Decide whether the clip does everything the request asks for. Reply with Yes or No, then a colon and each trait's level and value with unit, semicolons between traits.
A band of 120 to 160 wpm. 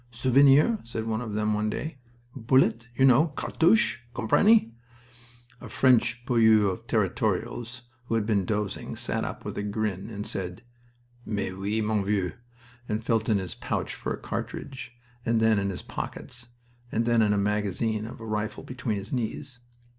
No: average, 170 wpm